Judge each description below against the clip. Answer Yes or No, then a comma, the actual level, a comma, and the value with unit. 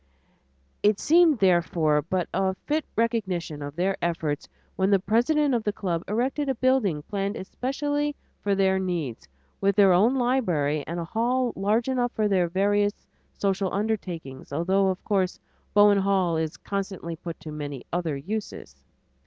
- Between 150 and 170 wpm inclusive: Yes, average, 155 wpm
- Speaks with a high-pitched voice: Yes, high, 195 Hz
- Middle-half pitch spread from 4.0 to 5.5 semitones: Yes, average, 4.7 semitones